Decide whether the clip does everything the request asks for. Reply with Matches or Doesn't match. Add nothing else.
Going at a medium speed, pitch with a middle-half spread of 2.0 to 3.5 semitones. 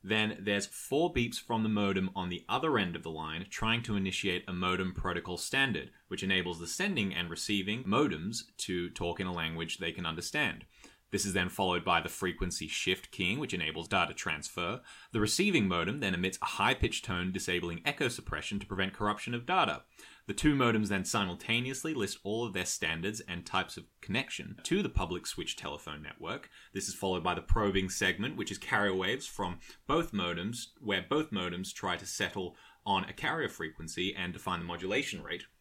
Matches